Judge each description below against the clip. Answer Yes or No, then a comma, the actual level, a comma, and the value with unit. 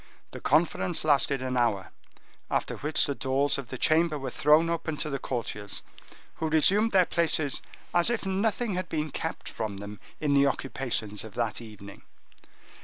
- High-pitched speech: No, medium, 140 Hz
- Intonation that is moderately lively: No, wide, 5.7 semitones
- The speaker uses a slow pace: No, average, 170 wpm